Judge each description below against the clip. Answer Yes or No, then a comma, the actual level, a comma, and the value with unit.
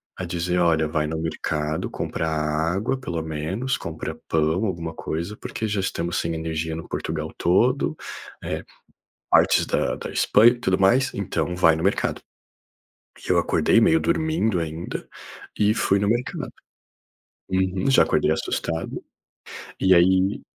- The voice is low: Yes, very low, 90 Hz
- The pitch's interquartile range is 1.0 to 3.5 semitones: No, average, 4.3 semitones